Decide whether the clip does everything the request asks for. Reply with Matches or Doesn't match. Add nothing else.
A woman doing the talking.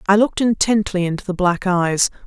Matches